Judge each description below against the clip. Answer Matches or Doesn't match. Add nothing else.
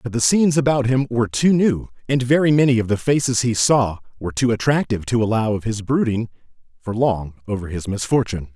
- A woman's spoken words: Doesn't match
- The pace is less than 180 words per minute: Doesn't match